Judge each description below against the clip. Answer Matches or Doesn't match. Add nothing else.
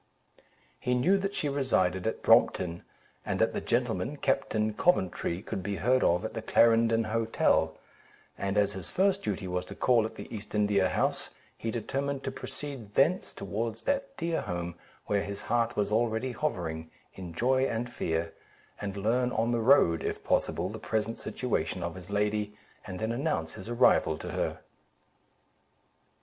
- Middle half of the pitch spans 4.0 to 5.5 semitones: Matches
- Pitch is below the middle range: Matches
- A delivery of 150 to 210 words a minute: Matches